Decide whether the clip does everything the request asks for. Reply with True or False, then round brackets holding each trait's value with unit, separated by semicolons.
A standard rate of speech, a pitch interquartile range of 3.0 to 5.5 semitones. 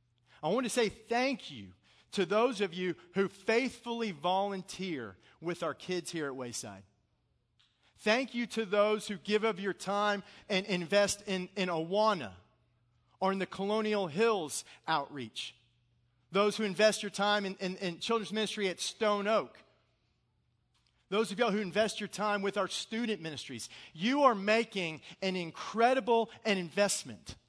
True (155 wpm; 5.2 semitones)